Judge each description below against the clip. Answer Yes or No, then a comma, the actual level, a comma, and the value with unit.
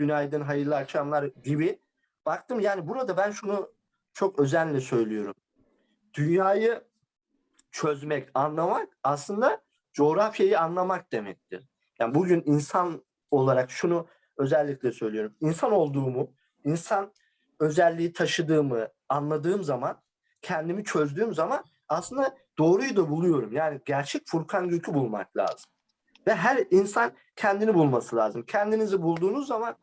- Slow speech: No, average, 110 wpm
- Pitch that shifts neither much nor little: No, wide, 5.7 semitones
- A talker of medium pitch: Yes, medium, 170 Hz